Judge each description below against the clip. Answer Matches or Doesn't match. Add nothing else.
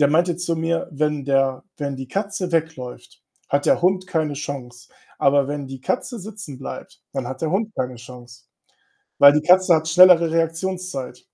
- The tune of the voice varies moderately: Matches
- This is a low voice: Doesn't match